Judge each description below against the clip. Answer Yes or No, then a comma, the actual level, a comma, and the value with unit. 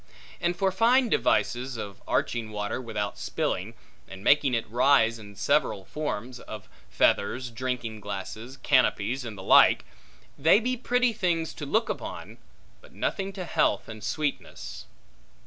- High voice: No, low, 125 Hz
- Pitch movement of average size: No, wide, 7.9 semitones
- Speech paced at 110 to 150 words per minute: Yes, average, 145 wpm